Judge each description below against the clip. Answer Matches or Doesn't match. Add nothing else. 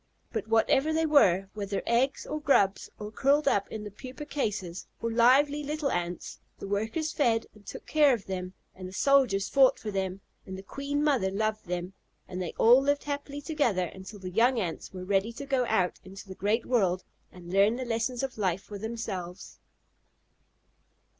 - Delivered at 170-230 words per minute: Matches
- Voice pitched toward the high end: Matches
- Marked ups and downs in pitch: Matches